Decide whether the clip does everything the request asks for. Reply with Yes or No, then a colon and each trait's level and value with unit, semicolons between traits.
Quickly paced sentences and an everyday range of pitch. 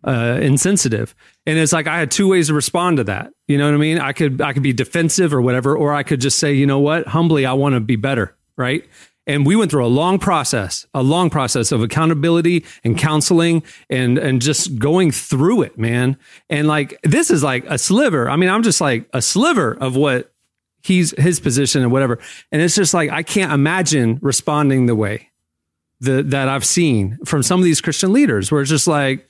Yes: fast, 220 wpm; average, 4.0 semitones